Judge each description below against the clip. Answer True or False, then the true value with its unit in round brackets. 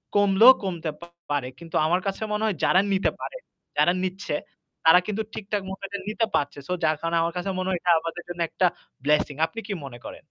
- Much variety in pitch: False (3.3 semitones)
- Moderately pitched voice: True (180 Hz)